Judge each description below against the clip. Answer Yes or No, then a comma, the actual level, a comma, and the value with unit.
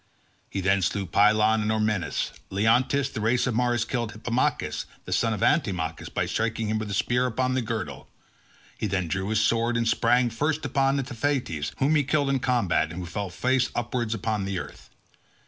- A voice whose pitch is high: No, low, 115 Hz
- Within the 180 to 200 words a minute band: Yes, average, 195 wpm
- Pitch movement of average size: Yes, average, 3.9 semitones